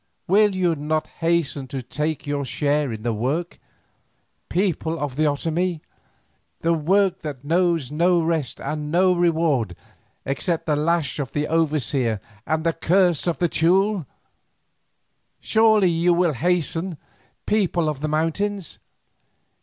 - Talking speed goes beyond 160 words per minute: No, slow, 135 wpm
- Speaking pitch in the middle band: Yes, medium, 165 Hz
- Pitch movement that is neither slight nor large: Yes, average, 3.2 semitones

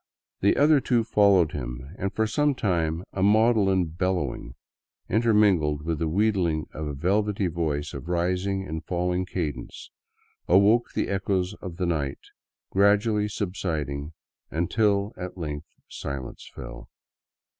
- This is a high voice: No, very low, 90 Hz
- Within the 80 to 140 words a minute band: Yes, slow, 135 wpm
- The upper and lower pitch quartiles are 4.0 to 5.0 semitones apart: Yes, average, 4.4 semitones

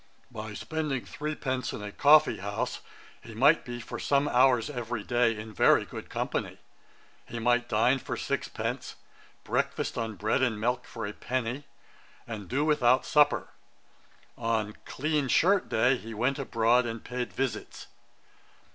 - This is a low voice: Yes, low, 120 Hz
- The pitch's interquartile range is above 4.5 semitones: No, average, 3.1 semitones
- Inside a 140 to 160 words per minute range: Yes, average, 155 wpm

